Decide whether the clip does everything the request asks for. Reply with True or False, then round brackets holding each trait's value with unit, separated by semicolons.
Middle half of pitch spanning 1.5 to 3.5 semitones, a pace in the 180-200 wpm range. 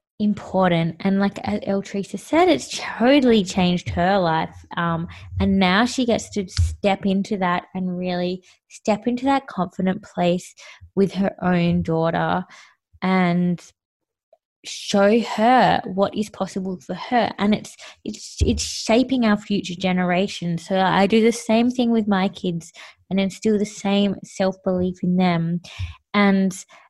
False (2.7 semitones; 145 wpm)